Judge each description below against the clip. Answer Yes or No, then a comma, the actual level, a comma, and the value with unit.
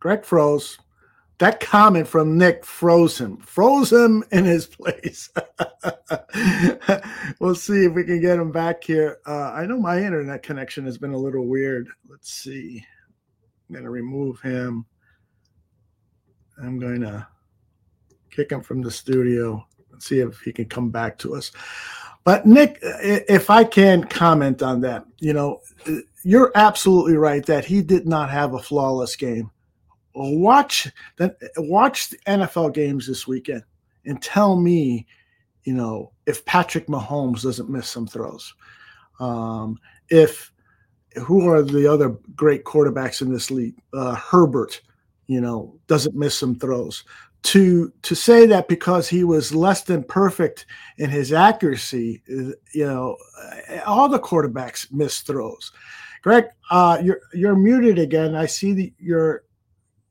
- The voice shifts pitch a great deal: Yes, wide, 6.2 semitones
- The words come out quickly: No, average, 145 wpm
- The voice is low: No, medium, 150 Hz